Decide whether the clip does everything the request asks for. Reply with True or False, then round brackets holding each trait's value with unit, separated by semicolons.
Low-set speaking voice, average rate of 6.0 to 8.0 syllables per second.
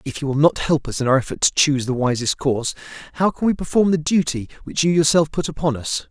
False (150 Hz; 6.3 syllables/s)